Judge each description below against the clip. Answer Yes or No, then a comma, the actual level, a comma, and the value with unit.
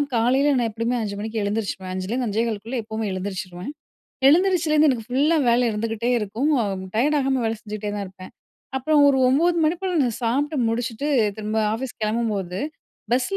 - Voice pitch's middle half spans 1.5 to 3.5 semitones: No, average, 4.2 semitones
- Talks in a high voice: Yes, high, 230 Hz